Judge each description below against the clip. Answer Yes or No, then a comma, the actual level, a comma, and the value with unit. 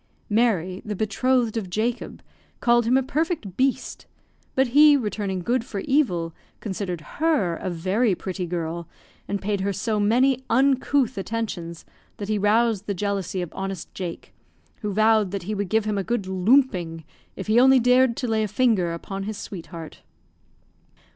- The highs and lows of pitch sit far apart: No, average, 4.4 semitones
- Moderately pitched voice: No, high, 210 Hz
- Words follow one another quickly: No, average, 165 wpm